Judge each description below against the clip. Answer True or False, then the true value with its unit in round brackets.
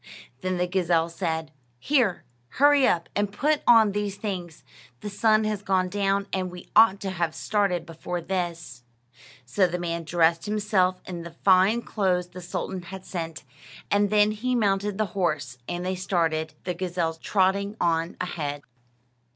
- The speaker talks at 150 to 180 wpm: True (160 wpm)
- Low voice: False (185 Hz)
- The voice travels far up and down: False (3.1 semitones)